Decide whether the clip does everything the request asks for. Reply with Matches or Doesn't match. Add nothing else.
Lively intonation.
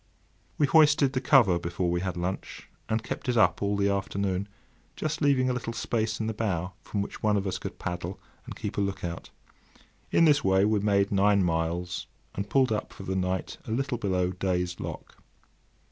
Doesn't match